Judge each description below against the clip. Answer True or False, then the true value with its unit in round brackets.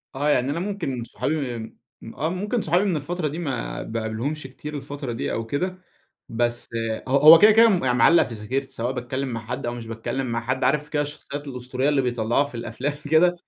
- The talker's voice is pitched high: False (135 Hz)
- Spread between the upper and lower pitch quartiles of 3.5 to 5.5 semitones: True (4.5 semitones)